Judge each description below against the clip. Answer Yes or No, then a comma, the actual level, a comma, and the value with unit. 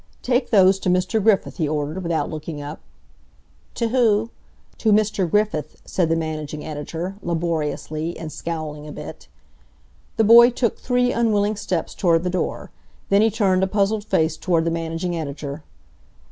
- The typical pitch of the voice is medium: Yes, medium, 175 Hz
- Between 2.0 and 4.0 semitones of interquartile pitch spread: No, average, 4.9 semitones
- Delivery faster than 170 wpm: No, average, 160 wpm